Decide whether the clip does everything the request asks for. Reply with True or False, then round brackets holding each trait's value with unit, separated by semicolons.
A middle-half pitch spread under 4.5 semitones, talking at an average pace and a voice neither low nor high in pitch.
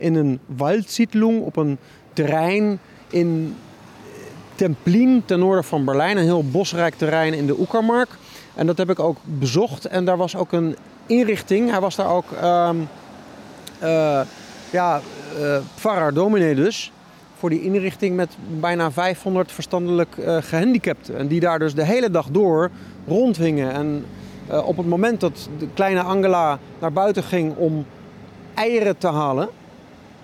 True (3.6 semitones; 150 wpm; 175 Hz)